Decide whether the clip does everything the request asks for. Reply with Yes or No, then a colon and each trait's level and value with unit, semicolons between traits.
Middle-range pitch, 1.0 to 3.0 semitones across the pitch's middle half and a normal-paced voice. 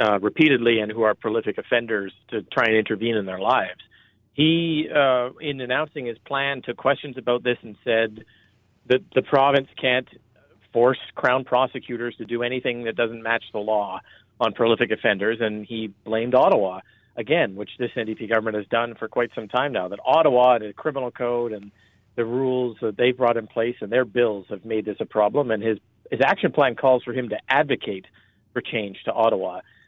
No: low, 120 Hz; narrow, 2.6 semitones; average, 195 wpm